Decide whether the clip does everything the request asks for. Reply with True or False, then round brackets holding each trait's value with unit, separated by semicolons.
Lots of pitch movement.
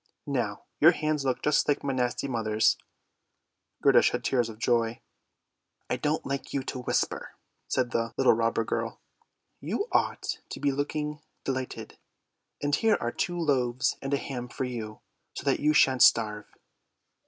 False (3.6 semitones)